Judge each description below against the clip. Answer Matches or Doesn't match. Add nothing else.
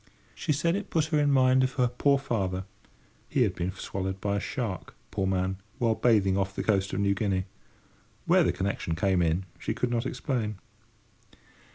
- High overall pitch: Doesn't match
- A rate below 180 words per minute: Doesn't match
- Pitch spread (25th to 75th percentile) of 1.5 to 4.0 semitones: Doesn't match